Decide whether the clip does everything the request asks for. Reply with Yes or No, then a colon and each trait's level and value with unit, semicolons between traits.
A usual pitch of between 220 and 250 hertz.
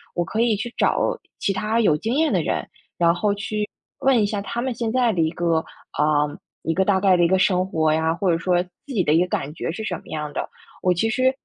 No: high, 190 Hz